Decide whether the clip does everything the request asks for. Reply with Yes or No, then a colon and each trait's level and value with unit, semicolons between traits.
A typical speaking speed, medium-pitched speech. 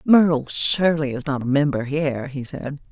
Yes: average, 185 wpm; medium, 145 Hz